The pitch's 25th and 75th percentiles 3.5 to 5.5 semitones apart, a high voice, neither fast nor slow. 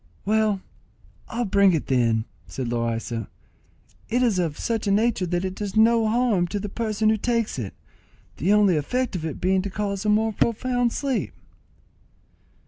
Yes: average, 4.2 semitones; high, 205 Hz; average, 170 wpm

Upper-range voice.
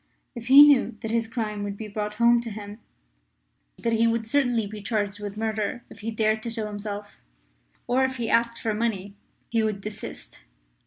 Yes: high, 220 Hz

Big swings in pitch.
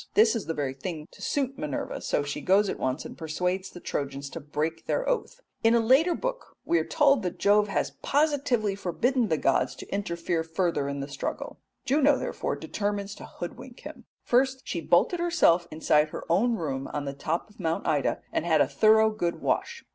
Yes: wide, 7.8 semitones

